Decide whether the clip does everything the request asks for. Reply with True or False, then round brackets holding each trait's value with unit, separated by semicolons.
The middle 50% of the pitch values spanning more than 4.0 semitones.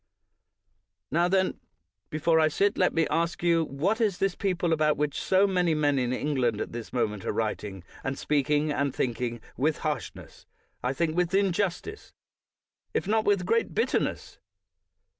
True (5.0 semitones)